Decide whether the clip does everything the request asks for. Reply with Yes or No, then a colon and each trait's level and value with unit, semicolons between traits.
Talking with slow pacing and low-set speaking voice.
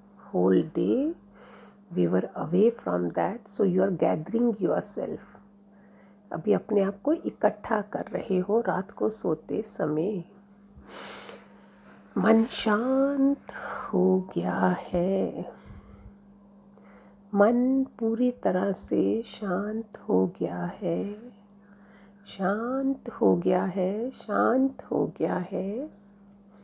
No: slow, 105 wpm; high, 200 Hz